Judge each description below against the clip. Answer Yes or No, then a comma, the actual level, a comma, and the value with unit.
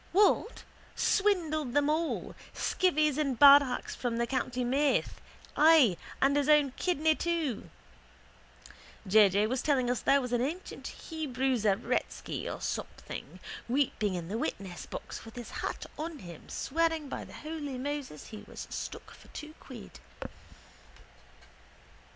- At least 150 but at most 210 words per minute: No, slow, 135 wpm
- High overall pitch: Yes, very high, 275 Hz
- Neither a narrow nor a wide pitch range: Yes, average, 4.3 semitones